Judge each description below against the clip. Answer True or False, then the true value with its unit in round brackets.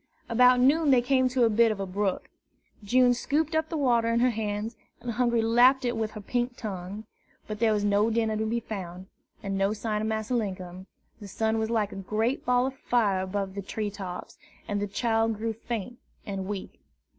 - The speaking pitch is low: False (220 Hz)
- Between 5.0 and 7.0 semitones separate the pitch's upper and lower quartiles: False (3.0 semitones)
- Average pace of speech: False (210 wpm)